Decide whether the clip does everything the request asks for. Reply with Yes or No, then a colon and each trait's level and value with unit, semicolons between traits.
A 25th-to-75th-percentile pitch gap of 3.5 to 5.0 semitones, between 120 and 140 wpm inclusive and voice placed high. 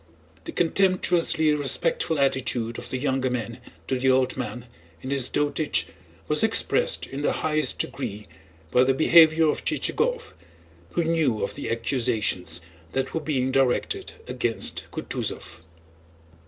No: average, 4.3 semitones; slow, 135 wpm; low, 135 Hz